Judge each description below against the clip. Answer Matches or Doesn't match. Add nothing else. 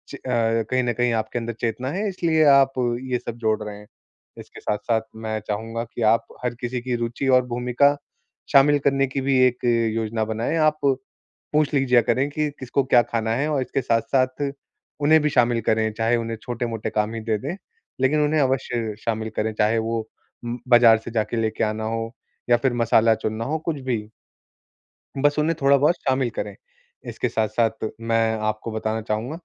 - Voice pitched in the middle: Doesn't match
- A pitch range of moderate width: Matches